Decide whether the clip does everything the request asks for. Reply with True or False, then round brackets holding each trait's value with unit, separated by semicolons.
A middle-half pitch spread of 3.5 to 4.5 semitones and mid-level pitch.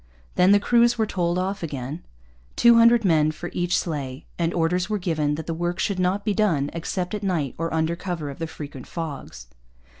True (3.8 semitones; 175 Hz)